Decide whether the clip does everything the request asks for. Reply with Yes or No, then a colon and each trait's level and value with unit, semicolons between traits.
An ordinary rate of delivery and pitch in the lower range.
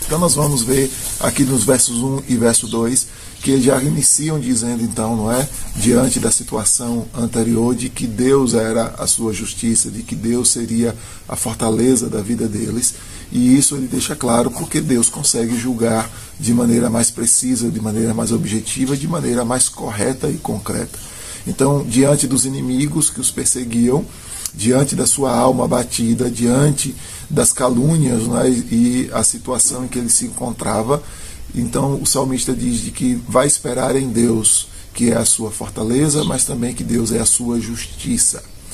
Yes: average, 165 wpm; low, 120 Hz